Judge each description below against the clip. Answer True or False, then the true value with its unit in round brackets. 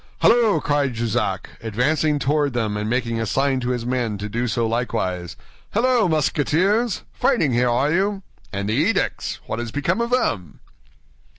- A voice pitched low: True (125 Hz)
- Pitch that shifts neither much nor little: False (5.8 semitones)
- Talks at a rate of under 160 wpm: False (165 wpm)